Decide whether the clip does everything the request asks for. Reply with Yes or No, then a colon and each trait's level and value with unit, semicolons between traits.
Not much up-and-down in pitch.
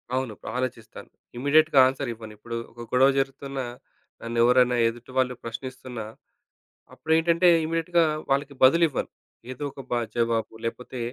No: average, 3.1 semitones